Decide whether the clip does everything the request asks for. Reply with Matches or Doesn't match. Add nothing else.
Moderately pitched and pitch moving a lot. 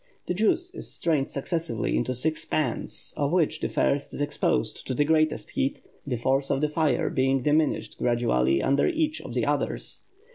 Doesn't match